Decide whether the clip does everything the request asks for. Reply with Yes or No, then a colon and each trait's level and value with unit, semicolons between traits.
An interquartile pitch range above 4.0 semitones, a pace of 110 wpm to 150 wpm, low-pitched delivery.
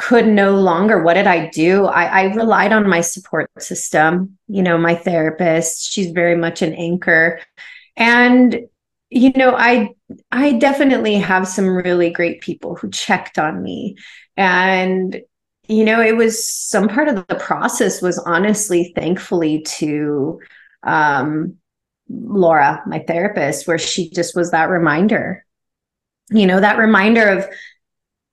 No: average, 4.6 semitones; average, 140 wpm; high, 190 Hz